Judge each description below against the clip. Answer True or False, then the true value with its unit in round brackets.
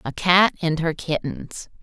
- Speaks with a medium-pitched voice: True (165 Hz)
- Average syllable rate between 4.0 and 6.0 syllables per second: False (3.8 syllables/s)